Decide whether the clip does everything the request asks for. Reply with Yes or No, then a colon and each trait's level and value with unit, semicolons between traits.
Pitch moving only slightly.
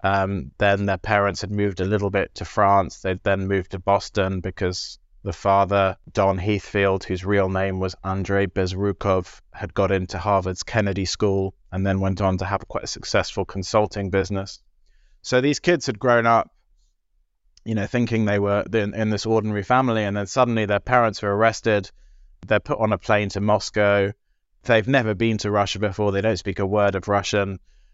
Yes: narrow, 1.7 semitones